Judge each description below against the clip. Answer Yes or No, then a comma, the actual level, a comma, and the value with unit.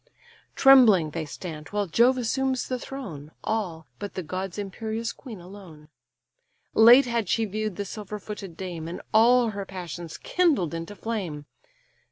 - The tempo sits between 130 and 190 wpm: Yes, average, 150 wpm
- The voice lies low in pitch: No, high, 205 Hz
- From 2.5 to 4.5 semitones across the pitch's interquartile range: No, average, 5.0 semitones